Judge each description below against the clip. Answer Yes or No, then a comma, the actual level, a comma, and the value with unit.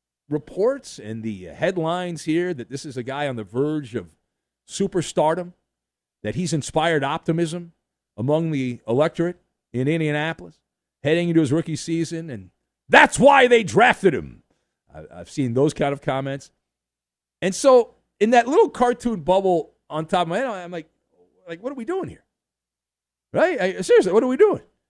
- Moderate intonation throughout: No, wide, 6.9 semitones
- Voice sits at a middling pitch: Yes, medium, 155 Hz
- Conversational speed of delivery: Yes, average, 165 wpm